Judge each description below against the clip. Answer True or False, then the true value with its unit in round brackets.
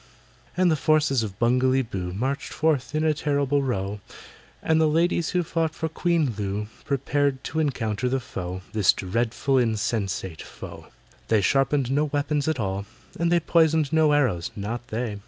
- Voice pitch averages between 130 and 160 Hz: True (135 Hz)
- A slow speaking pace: False (165 wpm)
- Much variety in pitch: True (6.0 semitones)